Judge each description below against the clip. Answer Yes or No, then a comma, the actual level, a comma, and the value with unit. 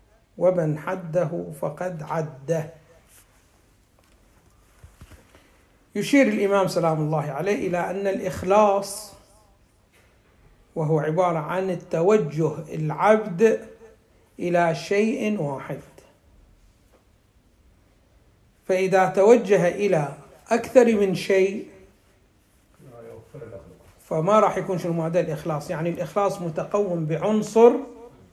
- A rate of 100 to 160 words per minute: No, average, 75 wpm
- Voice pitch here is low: No, medium, 165 Hz